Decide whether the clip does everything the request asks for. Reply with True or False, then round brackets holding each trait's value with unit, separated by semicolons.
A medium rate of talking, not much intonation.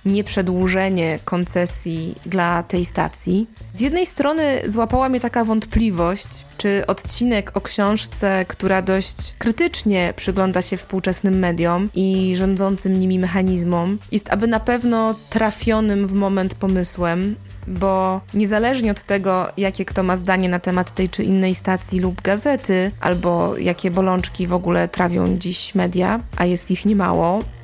True (135 wpm; 2.2 semitones)